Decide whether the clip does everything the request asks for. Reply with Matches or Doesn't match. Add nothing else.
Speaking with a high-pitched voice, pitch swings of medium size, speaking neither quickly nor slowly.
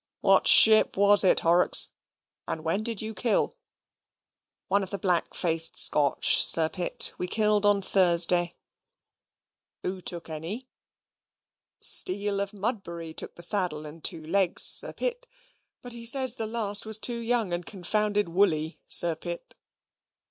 Matches